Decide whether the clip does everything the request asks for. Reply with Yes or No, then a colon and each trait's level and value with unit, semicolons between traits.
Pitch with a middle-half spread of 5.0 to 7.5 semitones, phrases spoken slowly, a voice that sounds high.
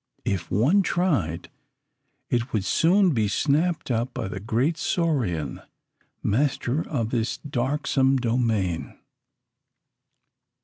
No: wide, 5.6 semitones; slow, 100 wpm; low, 125 Hz